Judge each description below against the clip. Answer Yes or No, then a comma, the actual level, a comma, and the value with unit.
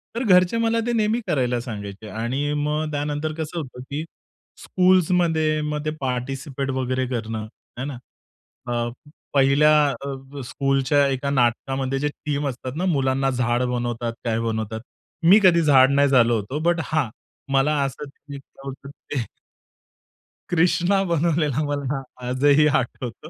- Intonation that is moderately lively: Yes, average, 3.5 semitones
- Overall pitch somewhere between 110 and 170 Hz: Yes, medium, 140 Hz